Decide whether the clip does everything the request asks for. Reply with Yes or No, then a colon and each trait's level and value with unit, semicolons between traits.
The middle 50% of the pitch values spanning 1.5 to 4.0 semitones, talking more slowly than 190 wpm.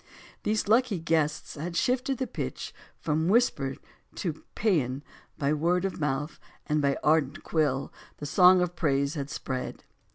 No: average, 4.4 semitones; average, 150 wpm